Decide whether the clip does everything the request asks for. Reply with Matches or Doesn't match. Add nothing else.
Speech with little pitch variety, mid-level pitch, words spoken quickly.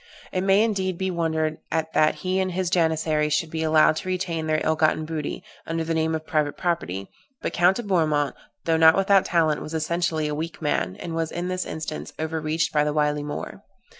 Matches